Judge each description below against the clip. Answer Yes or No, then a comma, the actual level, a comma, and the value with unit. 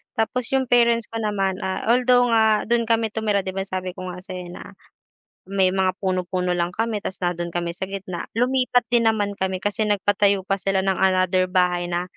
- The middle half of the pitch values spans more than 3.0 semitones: Yes, average, 3.4 semitones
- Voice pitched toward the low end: No, high, 195 Hz